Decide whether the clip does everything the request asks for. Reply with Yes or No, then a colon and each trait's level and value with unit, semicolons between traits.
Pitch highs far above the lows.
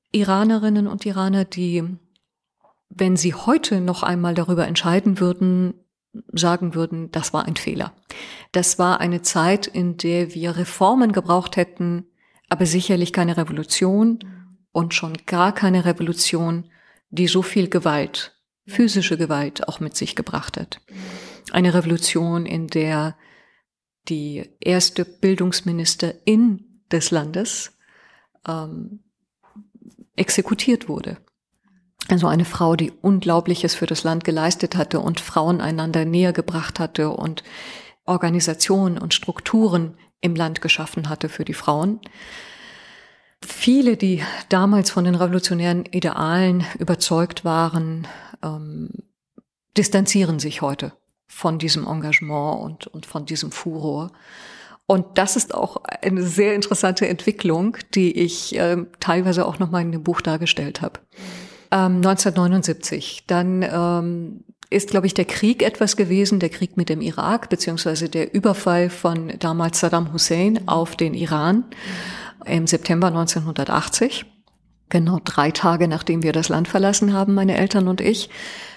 No: average, 2.7 semitones